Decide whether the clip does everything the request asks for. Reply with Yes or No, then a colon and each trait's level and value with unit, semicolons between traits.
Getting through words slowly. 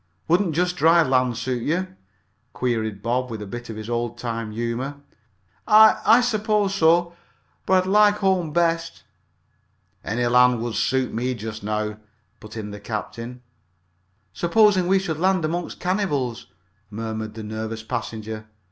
No: average, 145 wpm